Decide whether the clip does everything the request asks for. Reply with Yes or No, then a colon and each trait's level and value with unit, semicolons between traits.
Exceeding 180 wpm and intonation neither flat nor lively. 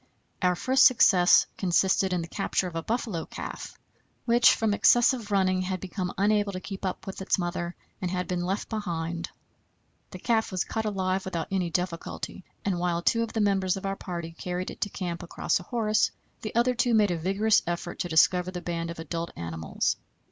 Yes: average, 200 wpm; average, 3.0 semitones